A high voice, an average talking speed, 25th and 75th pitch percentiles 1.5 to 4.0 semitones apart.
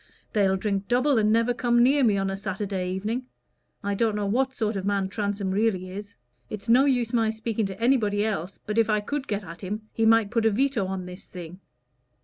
No: high, 210 Hz; fast, 220 wpm; average, 2.9 semitones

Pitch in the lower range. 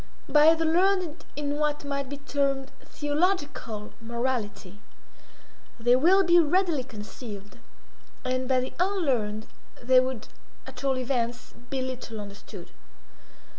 No: very high, 265 Hz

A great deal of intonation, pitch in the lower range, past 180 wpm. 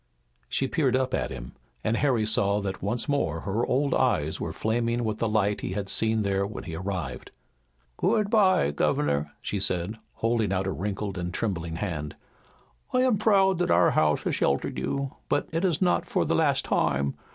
Yes: wide, 6.9 semitones; low, 105 Hz; average, 190 wpm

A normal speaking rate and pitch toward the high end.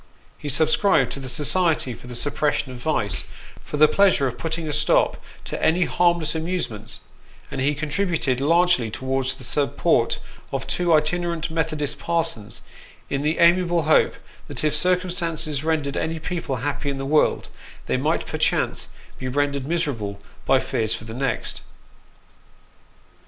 No: average, 160 wpm; medium, 150 Hz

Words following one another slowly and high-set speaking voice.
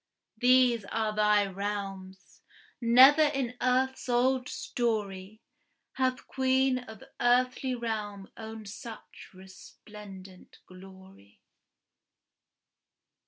Yes: slow, 80 wpm; high, 220 Hz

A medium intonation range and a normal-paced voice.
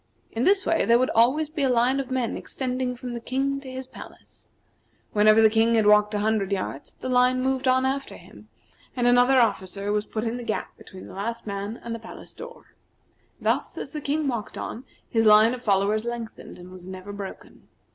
No: average, 3.6 semitones; fast, 210 wpm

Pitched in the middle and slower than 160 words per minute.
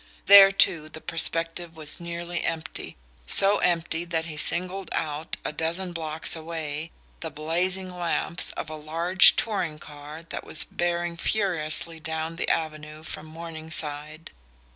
Yes: medium, 165 Hz; average, 140 wpm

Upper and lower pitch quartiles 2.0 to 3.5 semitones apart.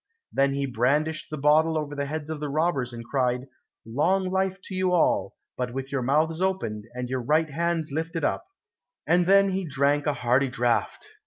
No: average, 4.0 semitones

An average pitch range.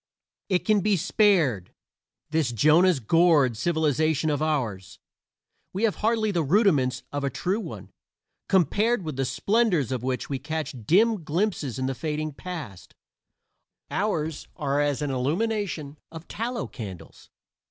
No: wide, 6.2 semitones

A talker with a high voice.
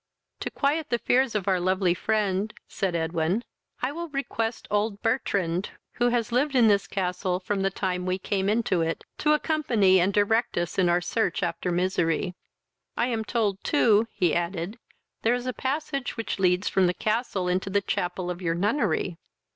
Yes: high, 200 Hz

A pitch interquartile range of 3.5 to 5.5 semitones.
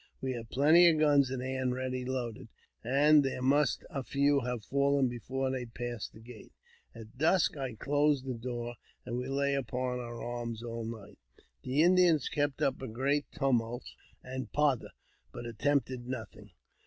No: average, 2.7 semitones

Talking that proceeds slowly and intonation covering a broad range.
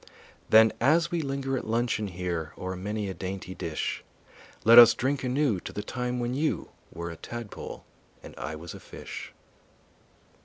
No: average, 165 wpm; wide, 5.8 semitones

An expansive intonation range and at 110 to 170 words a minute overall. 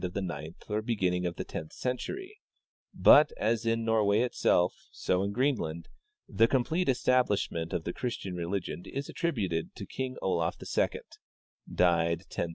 Yes: wide, 6.2 semitones; average, 160 wpm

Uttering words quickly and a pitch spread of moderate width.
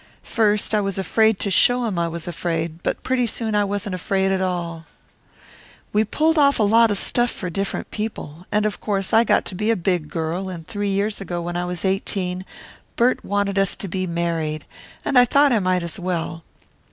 Yes: fast, 210 wpm; average, 3.4 semitones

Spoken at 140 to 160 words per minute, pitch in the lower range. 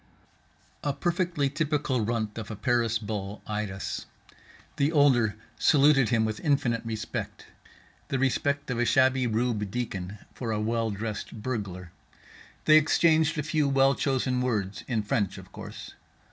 Yes: average, 145 wpm; low, 120 Hz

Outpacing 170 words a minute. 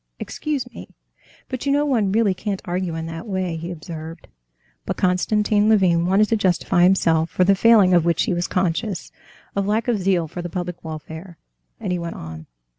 Yes: average, 190 wpm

